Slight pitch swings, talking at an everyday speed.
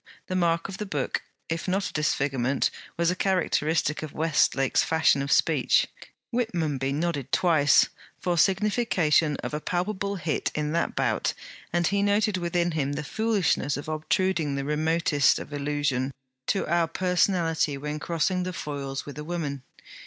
No: average, 3.8 semitones; average, 150 wpm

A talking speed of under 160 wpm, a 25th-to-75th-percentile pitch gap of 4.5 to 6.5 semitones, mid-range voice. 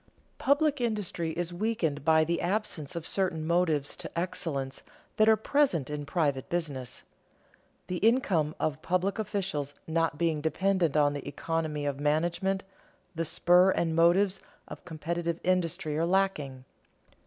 No: average, 140 wpm; average, 3.9 semitones; medium, 170 Hz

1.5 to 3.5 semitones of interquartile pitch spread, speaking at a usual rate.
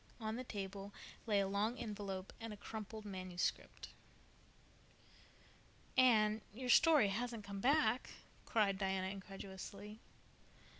No: narrow, 2.6 semitones; slow, 110 wpm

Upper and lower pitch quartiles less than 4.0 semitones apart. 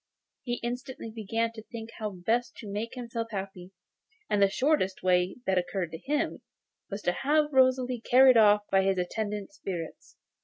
No: average, 4.3 semitones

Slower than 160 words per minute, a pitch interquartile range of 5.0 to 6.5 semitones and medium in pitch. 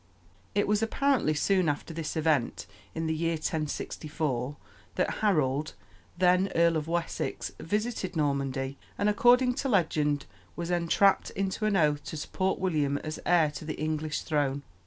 No: average, 150 wpm; average, 4.3 semitones; medium, 160 Hz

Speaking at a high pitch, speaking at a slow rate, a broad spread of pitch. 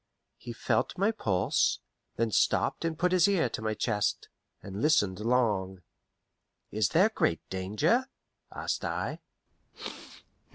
No: low, 115 Hz; slow, 125 wpm; wide, 9.0 semitones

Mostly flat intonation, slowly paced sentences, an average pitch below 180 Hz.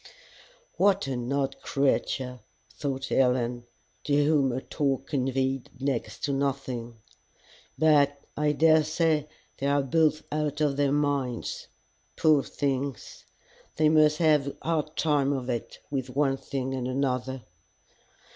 Yes: narrow, 2.2 semitones; slow, 130 wpm; medium, 140 Hz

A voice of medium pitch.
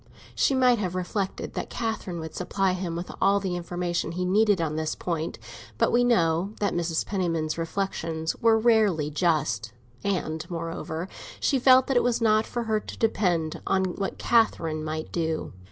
Yes: medium, 180 Hz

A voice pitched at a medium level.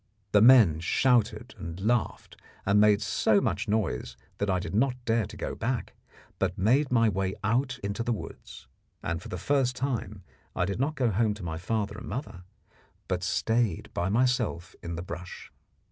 No: low, 105 Hz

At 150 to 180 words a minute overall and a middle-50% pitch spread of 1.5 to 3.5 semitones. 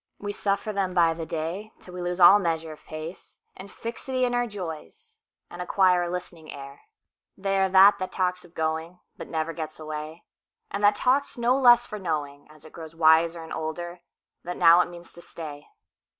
No: average, 165 wpm; average, 3.9 semitones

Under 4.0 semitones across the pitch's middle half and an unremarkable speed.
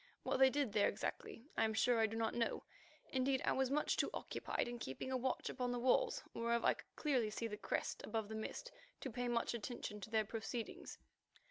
No: average, 2.8 semitones; fast, 220 wpm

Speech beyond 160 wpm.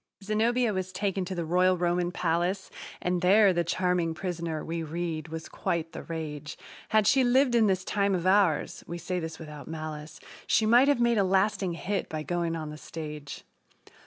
Yes: average, 190 wpm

